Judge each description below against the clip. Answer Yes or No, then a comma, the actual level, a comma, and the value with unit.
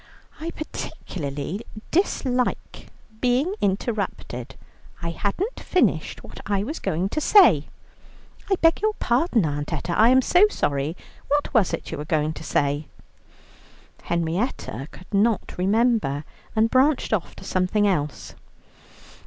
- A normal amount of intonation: No, wide, 8.4 semitones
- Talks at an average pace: No, slow, 130 wpm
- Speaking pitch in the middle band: No, high, 205 Hz